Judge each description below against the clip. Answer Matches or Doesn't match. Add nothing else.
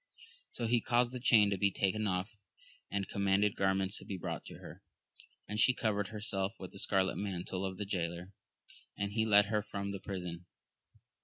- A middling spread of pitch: Doesn't match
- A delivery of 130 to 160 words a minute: Doesn't match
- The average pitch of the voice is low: Matches